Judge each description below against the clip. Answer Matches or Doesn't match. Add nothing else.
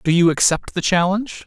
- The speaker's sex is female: Doesn't match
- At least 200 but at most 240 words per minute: Matches